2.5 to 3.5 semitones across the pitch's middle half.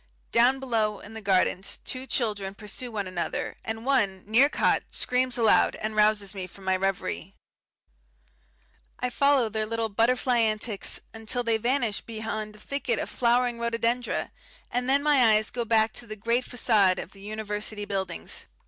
Yes: average, 2.9 semitones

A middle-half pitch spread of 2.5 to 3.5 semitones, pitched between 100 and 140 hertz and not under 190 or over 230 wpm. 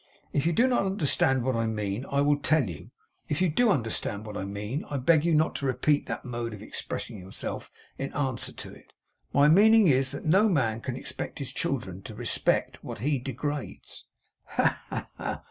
No: average, 5.2 semitones; low, 135 Hz; average, 200 wpm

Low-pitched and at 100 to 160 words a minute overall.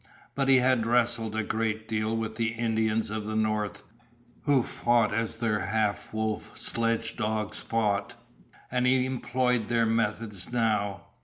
Yes: low, 115 Hz; average, 145 wpm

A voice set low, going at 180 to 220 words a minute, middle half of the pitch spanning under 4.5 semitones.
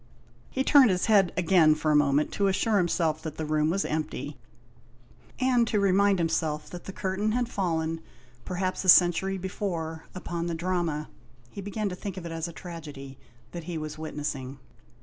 No: medium, 170 Hz; average, 190 wpm; average, 3.7 semitones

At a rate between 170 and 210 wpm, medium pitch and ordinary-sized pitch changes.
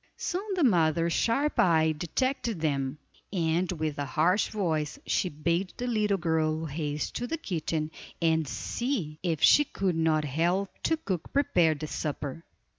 No: average, 155 wpm; medium, 165 Hz; average, 4.3 semitones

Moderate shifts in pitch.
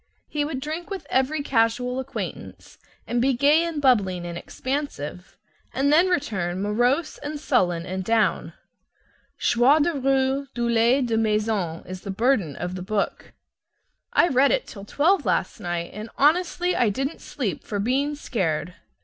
No: wide, 6.4 semitones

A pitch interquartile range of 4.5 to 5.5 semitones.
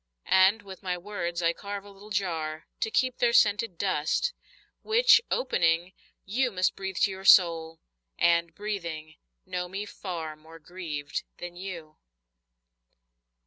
No: average, 3.5 semitones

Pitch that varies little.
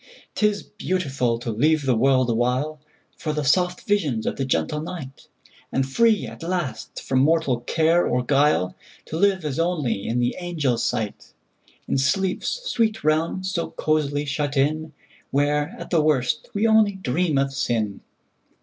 No: average, 5.1 semitones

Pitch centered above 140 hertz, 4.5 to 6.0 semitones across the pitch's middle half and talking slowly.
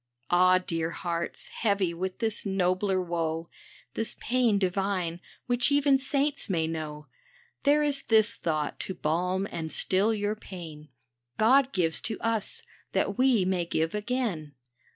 No: high, 190 Hz; average, 5.2 semitones; average, 145 wpm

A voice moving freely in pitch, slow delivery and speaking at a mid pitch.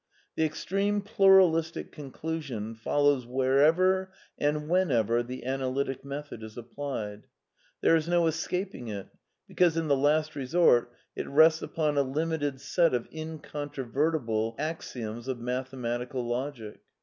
No: average, 4.6 semitones; slow, 125 wpm; medium, 145 Hz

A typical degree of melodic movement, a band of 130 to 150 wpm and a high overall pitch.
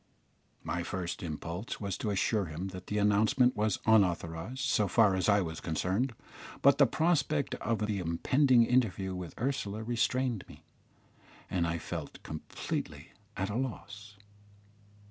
No: average, 5.0 semitones; average, 145 wpm; low, 105 Hz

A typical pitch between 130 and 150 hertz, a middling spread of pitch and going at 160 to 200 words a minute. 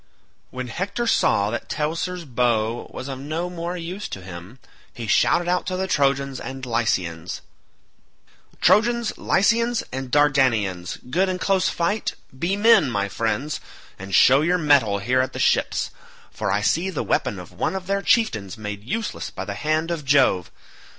No: medium, 140 Hz; wide, 8.2 semitones; average, 165 wpm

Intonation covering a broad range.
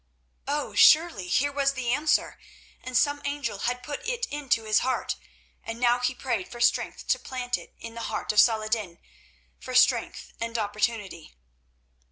No: average, 3.9 semitones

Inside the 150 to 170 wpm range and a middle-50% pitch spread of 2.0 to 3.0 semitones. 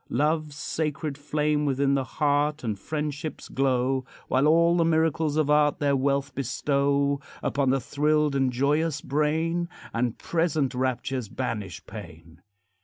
No: slow, 135 wpm; narrow, 2.4 semitones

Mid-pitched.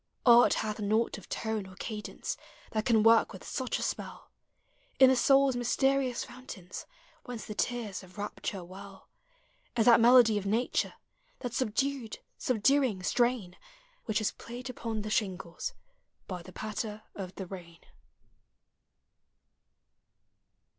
No: high, 220 Hz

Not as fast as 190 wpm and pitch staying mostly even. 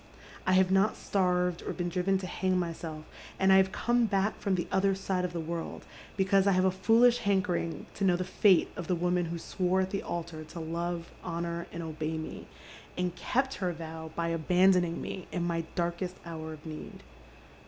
No: average, 200 wpm; narrow, 2.2 semitones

